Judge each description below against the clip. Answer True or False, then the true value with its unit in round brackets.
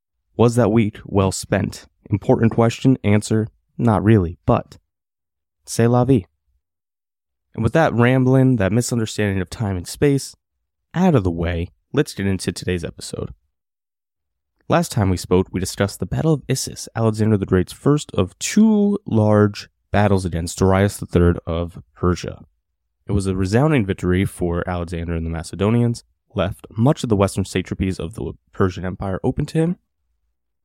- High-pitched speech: False (95 Hz)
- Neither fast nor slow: True (155 wpm)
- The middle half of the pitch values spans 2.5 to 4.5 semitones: False (5.2 semitones)